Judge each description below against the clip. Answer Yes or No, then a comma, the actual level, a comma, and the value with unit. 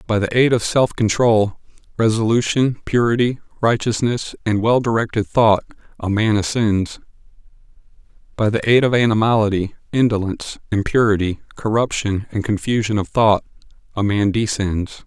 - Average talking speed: No, slow, 125 wpm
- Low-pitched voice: Yes, low, 110 Hz